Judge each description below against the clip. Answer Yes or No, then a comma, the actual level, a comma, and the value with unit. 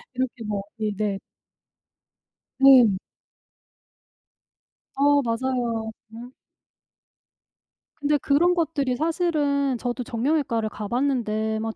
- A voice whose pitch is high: Yes, very high, 250 Hz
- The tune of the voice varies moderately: Yes, average, 4.2 semitones